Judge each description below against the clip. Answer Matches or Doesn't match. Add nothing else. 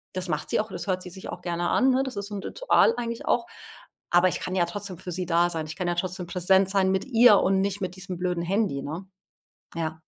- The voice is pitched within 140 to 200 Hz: Matches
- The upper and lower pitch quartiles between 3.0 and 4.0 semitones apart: Doesn't match